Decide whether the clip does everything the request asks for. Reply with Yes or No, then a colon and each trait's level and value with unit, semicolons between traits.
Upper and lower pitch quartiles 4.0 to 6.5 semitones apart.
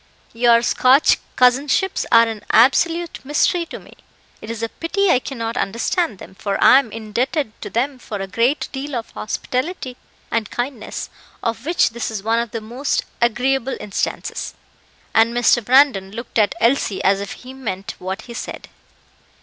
No: average, 3.5 semitones